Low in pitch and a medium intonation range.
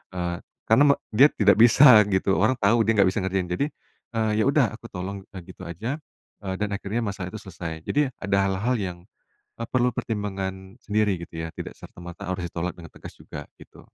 Yes: low, 100 Hz; average, 3.5 semitones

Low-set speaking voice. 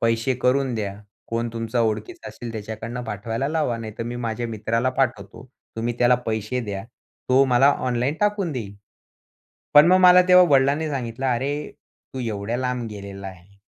Yes: low, 120 Hz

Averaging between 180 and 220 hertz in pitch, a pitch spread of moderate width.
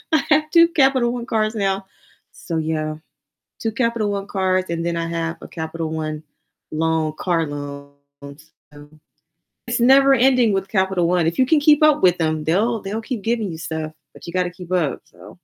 No: medium, 185 Hz; wide, 6.4 semitones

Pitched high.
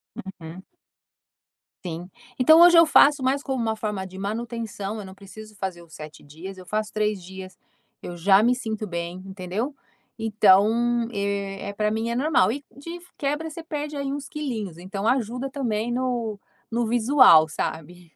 Yes: high, 215 Hz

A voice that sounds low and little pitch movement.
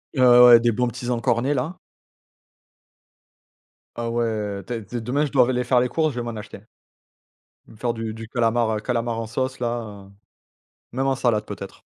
Yes: low, 120 Hz; narrow, 1.9 semitones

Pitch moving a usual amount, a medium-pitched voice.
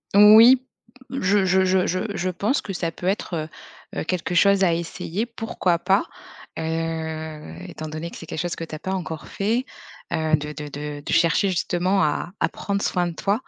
Yes: average, 3.6 semitones; medium, 175 Hz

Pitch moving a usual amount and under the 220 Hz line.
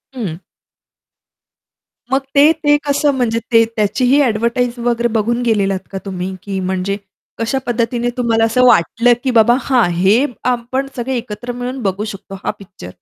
No: average, 3.7 semitones; high, 235 Hz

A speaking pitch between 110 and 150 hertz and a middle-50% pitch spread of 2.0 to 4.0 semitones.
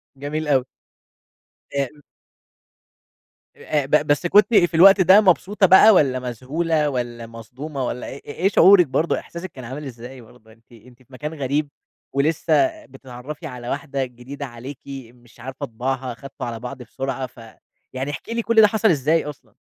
No: medium, 140 Hz; average, 4.7 semitones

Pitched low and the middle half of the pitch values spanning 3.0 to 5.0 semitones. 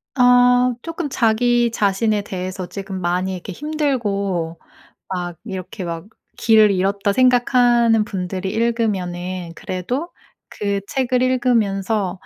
No: high, 205 Hz; average, 4.7 semitones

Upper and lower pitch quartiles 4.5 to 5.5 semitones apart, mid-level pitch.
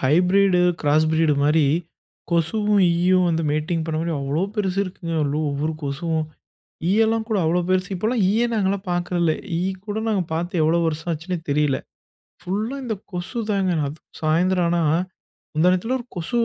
No: average, 3.8 semitones; medium, 175 Hz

